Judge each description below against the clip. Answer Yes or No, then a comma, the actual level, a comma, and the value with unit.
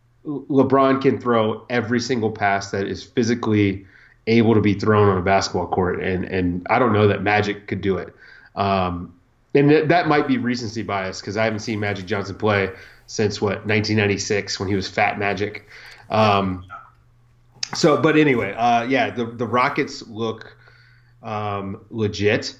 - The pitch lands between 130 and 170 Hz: No, low, 110 Hz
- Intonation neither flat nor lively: Yes, average, 3.4 semitones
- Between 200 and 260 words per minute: No, average, 165 wpm